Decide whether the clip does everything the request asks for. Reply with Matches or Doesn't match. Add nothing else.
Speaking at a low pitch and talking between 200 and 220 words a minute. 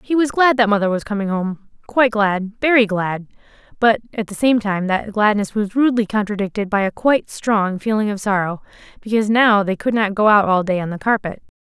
Doesn't match